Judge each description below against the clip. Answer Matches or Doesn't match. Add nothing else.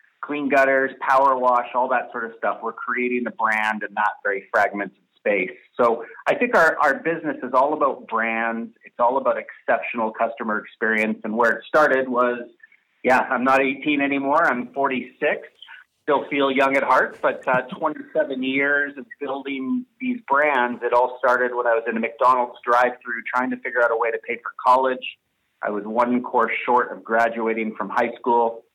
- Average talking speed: Matches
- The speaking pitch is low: Matches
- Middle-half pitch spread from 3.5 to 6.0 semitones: Doesn't match